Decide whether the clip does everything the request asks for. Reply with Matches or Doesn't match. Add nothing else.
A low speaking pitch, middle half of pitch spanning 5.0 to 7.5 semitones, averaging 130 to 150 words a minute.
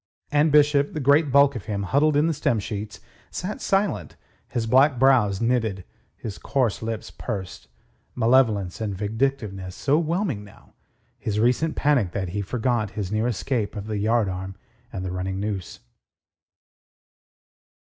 Matches